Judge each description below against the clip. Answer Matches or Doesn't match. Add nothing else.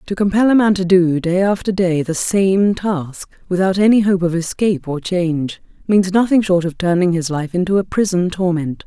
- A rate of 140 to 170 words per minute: Doesn't match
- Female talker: Matches